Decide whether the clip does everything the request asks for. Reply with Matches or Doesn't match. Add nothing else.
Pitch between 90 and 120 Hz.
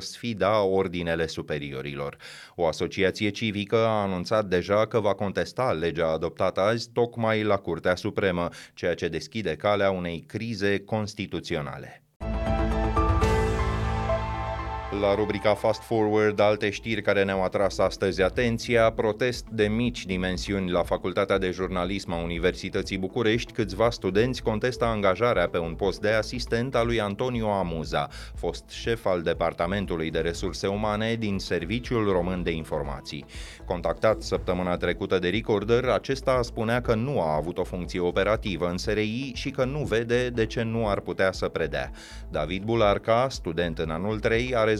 Matches